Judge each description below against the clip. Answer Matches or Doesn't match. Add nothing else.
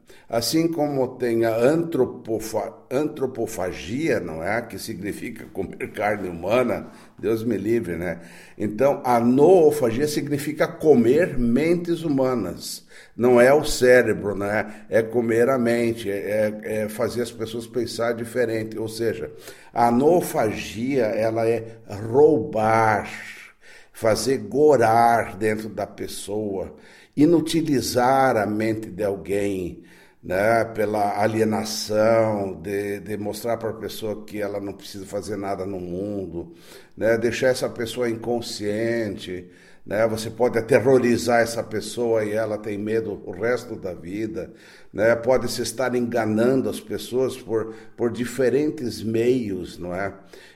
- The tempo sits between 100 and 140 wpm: Matches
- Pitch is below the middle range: Matches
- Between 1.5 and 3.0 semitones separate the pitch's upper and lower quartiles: Matches